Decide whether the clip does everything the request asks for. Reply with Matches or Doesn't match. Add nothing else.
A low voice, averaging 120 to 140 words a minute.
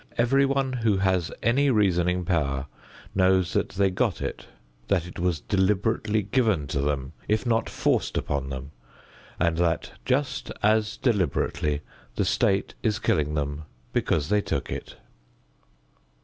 Matches